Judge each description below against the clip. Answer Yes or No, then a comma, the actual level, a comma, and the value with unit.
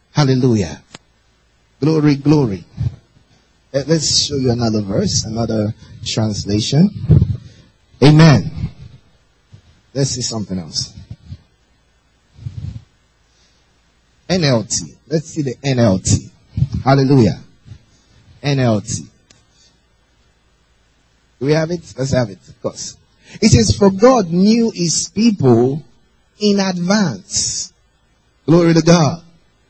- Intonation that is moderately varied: No, wide, 6.4 semitones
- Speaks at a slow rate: Yes, slow, 85 wpm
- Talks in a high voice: No, low, 125 Hz